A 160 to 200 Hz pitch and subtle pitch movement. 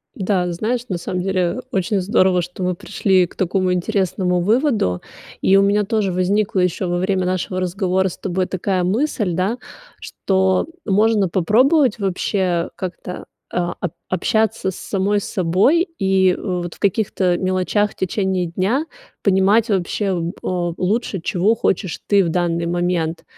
Yes: high, 190 Hz; narrow, 2.3 semitones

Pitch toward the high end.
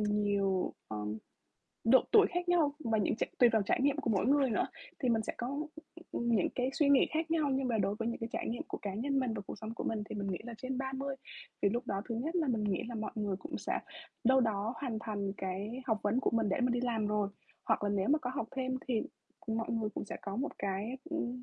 Yes: high, 230 Hz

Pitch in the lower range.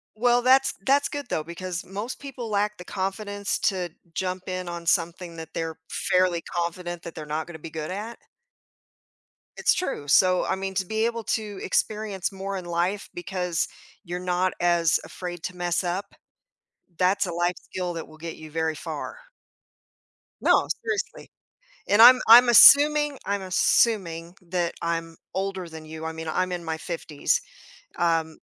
No: medium, 180 Hz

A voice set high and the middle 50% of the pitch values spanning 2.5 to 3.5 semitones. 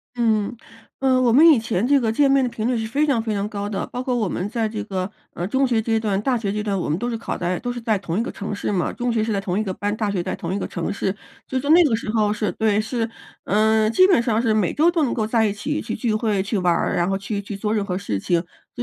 Yes: high, 220 Hz; average, 3.2 semitones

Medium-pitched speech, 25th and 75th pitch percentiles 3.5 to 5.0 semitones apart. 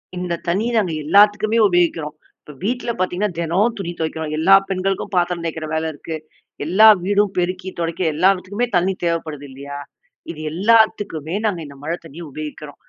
Yes: medium, 175 Hz; average, 3.8 semitones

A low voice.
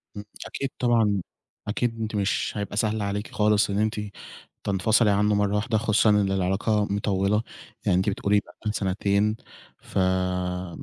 Yes: low, 105 Hz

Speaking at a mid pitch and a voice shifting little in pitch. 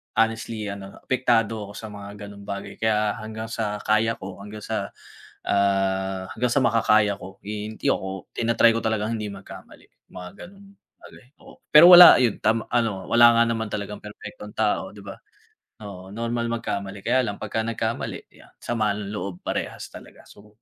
No: low, 105 Hz; narrow, 2.3 semitones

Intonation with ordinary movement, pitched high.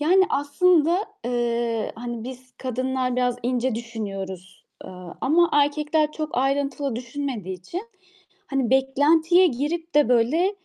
Yes: average, 4.2 semitones; very high, 265 Hz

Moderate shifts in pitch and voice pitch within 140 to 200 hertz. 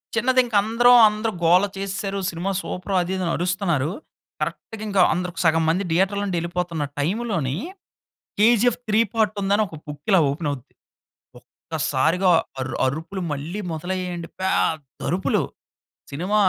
Yes: average, 3.9 semitones; medium, 185 Hz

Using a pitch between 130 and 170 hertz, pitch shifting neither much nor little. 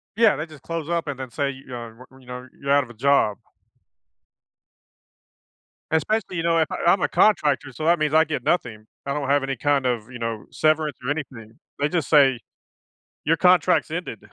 Yes: medium, 140 Hz; average, 4.0 semitones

